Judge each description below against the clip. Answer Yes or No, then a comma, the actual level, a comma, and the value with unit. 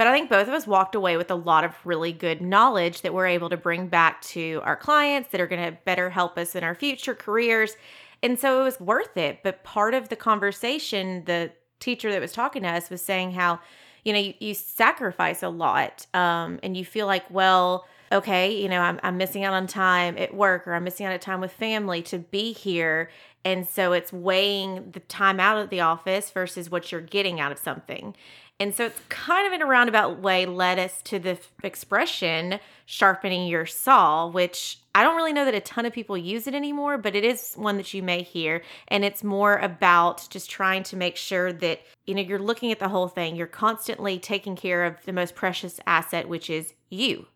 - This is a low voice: No, high, 190 Hz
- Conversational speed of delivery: No, fast, 220 wpm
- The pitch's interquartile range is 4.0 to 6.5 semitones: No, average, 3.0 semitones